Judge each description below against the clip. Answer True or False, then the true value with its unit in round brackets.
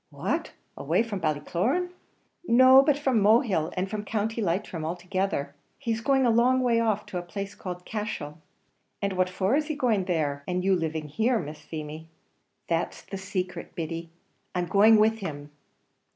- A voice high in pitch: True (195 Hz)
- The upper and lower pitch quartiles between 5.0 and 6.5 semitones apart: True (5.4 semitones)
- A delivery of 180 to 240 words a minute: False (165 wpm)